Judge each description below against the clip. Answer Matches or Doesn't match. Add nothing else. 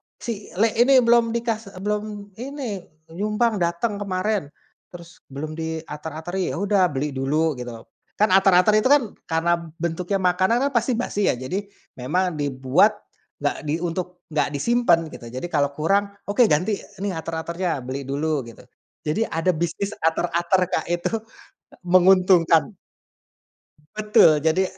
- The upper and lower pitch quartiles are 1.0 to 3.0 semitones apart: Doesn't match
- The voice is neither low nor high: Matches